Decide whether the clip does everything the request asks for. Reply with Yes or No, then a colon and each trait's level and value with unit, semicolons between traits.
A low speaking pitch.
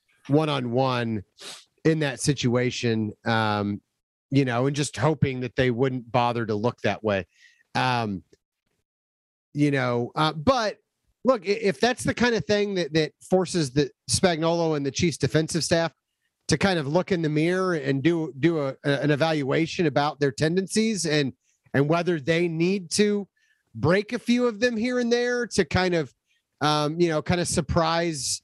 No: medium, 155 Hz